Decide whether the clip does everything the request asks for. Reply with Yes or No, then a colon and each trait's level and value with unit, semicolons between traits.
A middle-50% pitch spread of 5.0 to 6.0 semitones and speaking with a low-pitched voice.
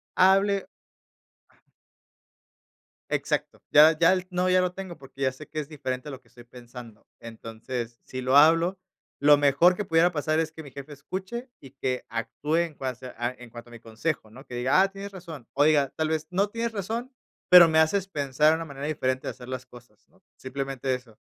No: wide, 5.6 semitones; medium, 145 Hz